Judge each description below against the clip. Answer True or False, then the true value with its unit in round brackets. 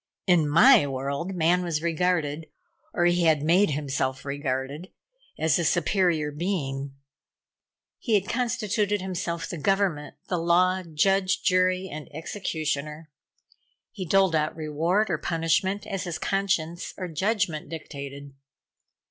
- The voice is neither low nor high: True (170 Hz)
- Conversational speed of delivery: False (125 wpm)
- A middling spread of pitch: True (3.8 semitones)